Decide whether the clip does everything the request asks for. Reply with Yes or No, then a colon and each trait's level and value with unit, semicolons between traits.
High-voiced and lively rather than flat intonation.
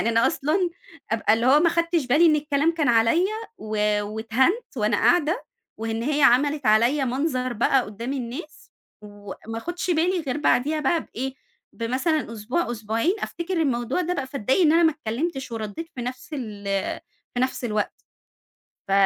Yes: very high, 265 Hz; wide, 5.7 semitones